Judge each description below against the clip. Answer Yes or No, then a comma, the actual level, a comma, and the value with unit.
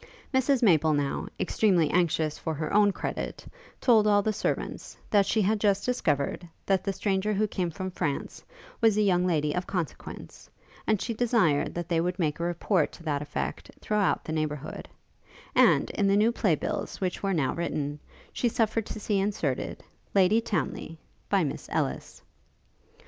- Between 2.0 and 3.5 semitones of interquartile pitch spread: No, average, 4.9 semitones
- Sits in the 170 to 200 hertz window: Yes, medium, 185 Hz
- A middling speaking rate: Yes, average, 170 wpm